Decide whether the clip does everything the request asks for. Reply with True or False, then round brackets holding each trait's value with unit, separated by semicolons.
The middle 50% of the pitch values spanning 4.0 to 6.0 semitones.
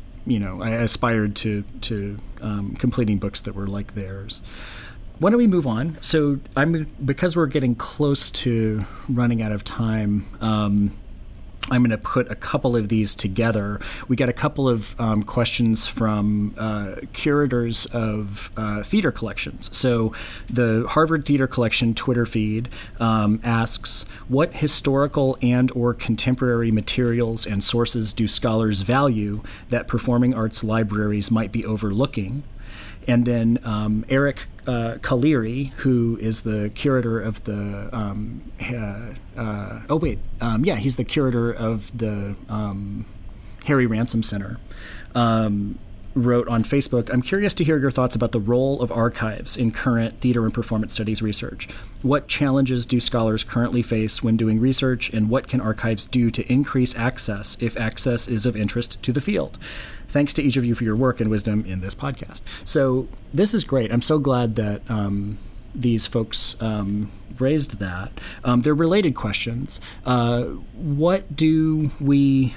False (3.2 semitones)